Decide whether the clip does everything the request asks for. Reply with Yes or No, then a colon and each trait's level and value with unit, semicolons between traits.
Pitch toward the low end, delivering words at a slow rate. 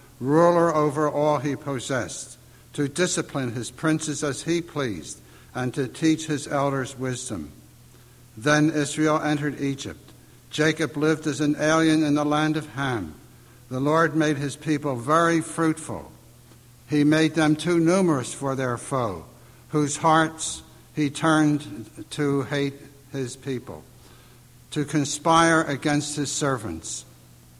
No: medium, 145 Hz; slow, 130 wpm